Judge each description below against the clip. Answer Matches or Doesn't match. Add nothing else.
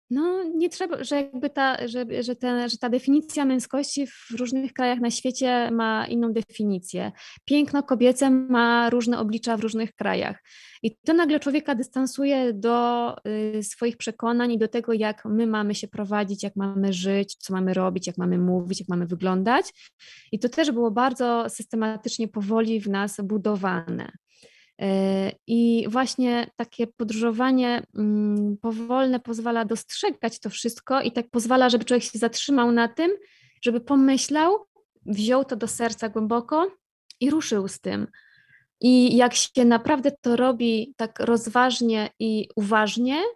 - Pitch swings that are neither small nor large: Matches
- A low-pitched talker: Doesn't match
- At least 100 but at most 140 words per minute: Doesn't match